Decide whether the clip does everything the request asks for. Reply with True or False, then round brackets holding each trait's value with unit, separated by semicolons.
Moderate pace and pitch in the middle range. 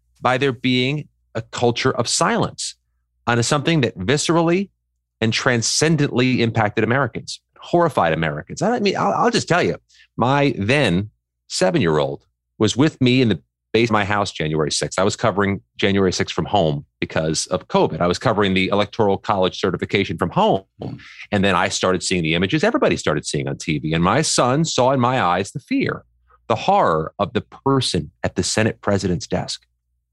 False (180 wpm; 105 Hz)